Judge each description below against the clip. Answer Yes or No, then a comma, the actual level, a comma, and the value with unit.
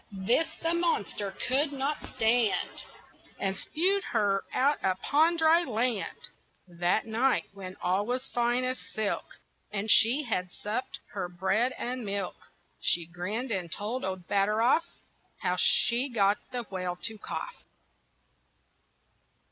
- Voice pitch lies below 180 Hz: No, high, 225 Hz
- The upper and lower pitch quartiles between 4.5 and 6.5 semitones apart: Yes, average, 4.8 semitones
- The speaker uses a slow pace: Yes, slow, 130 wpm